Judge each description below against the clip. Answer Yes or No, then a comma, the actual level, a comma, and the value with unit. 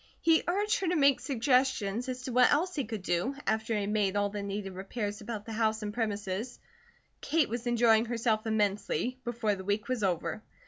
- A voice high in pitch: Yes, high, 220 Hz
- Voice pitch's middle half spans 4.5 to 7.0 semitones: No, average, 3.7 semitones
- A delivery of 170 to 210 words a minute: Yes, average, 200 wpm